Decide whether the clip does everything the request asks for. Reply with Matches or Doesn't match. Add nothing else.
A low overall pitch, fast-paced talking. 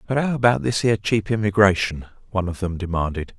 Doesn't match